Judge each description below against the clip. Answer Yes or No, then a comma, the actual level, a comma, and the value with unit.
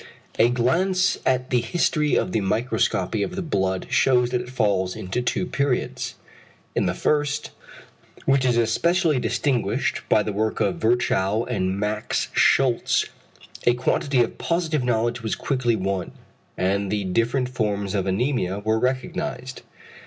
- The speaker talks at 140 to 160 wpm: Yes, average, 145 wpm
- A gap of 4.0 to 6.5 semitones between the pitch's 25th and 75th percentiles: Yes, average, 4.3 semitones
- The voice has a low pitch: Yes, low, 120 Hz